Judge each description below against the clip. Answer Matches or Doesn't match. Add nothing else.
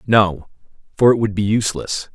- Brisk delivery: Doesn't match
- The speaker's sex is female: Doesn't match